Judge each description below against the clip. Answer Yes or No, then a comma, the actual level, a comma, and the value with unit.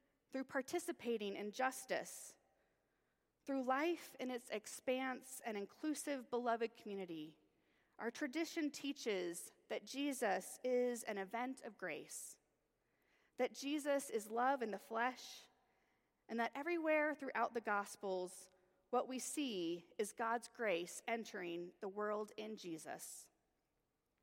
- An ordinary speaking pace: No, slow, 115 wpm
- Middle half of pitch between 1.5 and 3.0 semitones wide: No, average, 4.3 semitones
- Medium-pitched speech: No, high, 235 Hz